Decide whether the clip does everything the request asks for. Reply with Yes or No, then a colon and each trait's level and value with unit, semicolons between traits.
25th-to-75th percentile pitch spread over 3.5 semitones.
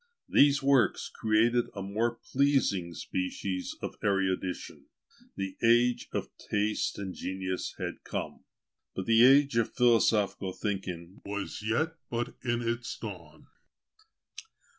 Yes: average, 4.0 semitones